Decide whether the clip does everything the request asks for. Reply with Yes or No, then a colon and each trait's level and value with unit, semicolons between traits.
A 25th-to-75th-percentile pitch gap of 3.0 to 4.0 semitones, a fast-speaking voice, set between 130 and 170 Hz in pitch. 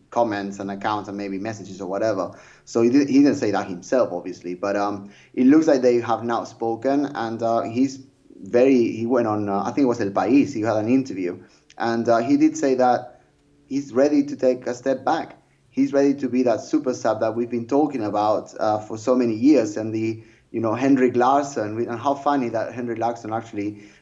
No: average, 3.7 semitones; fast, 215 wpm; low, 115 Hz